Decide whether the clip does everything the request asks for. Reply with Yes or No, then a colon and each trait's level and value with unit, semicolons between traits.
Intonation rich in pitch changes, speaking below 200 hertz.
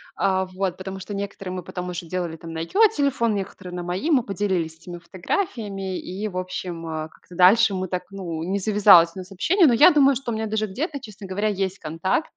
No: average, 3.2 semitones; high, 190 Hz